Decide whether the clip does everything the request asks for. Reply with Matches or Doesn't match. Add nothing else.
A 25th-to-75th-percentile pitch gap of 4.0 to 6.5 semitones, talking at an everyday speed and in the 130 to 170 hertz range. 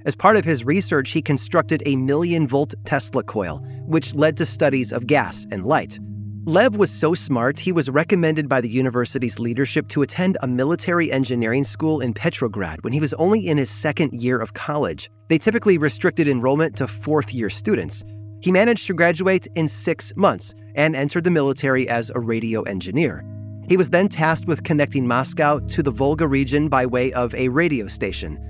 Matches